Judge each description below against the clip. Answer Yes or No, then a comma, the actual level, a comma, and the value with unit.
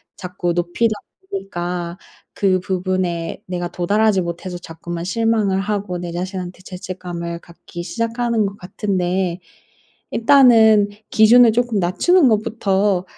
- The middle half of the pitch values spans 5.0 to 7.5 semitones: No, average, 3.6 semitones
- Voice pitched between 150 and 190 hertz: Yes, medium, 185 Hz